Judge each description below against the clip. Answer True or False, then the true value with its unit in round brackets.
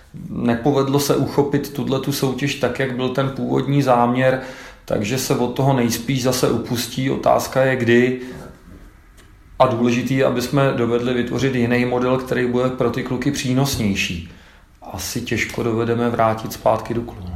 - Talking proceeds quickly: False (150 wpm)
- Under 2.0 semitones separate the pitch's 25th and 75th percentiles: False (2.3 semitones)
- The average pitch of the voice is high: False (125 Hz)